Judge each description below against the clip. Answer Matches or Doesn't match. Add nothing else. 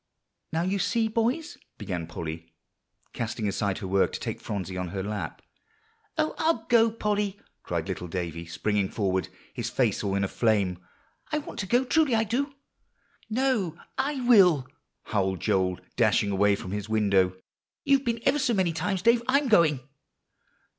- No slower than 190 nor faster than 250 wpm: Doesn't match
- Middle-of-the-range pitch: Matches